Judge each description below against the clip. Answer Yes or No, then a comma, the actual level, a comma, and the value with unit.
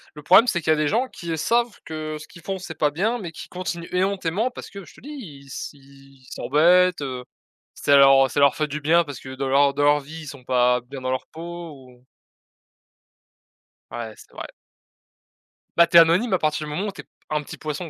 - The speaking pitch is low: No, medium, 155 Hz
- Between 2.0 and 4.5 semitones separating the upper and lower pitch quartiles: Yes, average, 4.0 semitones